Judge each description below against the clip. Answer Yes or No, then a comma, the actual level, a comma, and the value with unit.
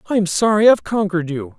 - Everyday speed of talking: Yes, average, 190 wpm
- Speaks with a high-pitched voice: No, medium, 180 Hz